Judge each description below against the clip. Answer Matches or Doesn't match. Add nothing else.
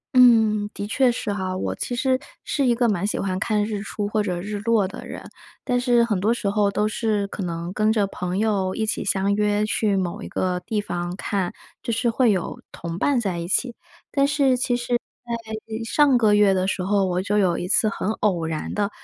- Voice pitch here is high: Matches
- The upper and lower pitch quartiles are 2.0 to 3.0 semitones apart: Doesn't match